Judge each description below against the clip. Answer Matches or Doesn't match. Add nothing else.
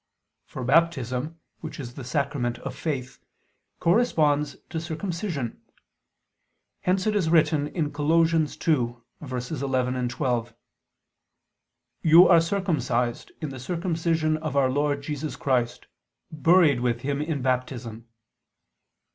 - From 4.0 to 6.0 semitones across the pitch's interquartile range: Matches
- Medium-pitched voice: Matches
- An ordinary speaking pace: Doesn't match